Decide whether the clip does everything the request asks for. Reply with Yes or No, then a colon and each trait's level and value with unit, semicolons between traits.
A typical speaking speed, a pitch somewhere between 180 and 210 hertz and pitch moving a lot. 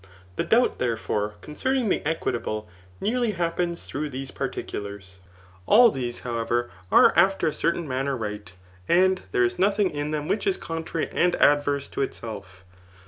No: average, 150 wpm; medium, 145 Hz; wide, 7.4 semitones